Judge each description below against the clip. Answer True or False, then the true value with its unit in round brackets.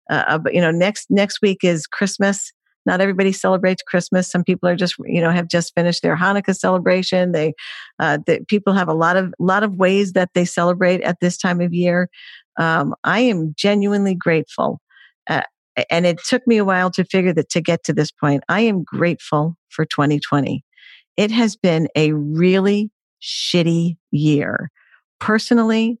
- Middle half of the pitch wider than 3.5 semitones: False (3.0 semitones)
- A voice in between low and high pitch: True (180 Hz)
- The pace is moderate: True (175 wpm)